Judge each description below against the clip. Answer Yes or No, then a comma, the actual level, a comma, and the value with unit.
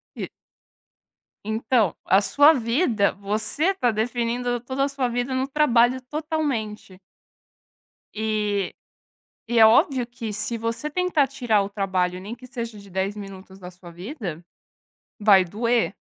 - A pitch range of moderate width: Yes, average, 4.1 semitones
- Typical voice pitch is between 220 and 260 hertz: Yes, high, 230 Hz